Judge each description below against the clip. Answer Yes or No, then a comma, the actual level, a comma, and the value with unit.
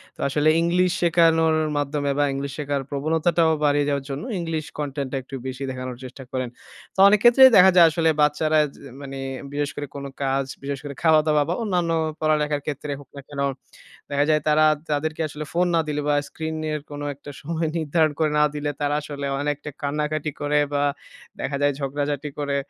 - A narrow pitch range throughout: Yes, narrow, 1.9 semitones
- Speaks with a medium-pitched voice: Yes, medium, 150 Hz